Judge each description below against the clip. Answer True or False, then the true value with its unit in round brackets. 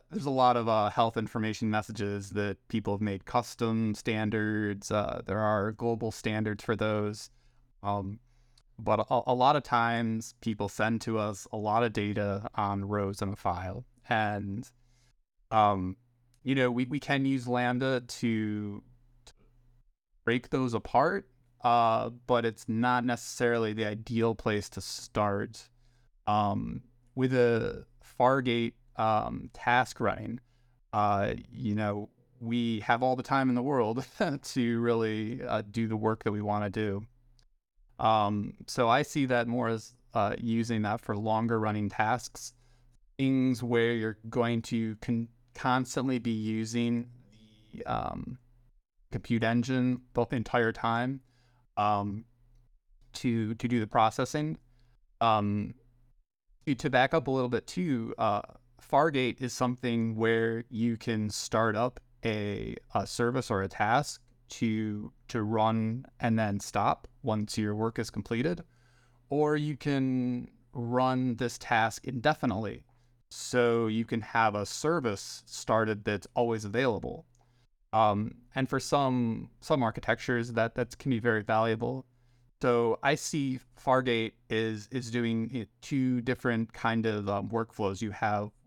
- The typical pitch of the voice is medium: False (115 Hz)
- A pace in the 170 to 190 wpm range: False (145 wpm)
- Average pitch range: False (2.1 semitones)